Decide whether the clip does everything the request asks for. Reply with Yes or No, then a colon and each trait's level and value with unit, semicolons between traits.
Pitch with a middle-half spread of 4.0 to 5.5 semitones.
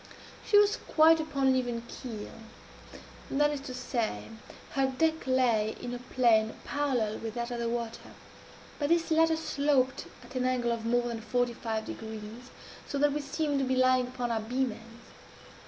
No: average, 3.3 semitones